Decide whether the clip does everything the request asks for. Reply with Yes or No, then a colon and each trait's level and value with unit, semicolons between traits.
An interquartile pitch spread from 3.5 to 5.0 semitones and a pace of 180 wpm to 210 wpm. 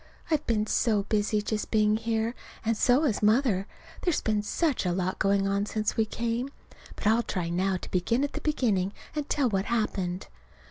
No: average, 3.1 semitones; average, 190 wpm